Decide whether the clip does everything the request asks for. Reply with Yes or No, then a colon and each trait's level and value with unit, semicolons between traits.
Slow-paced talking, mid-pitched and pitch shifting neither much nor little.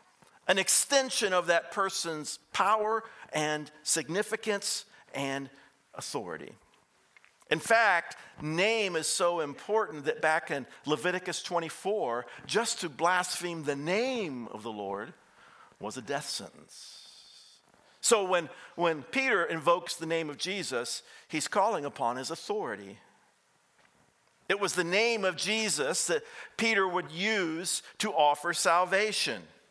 Yes: slow, 120 wpm; medium, 180 Hz; average, 4.7 semitones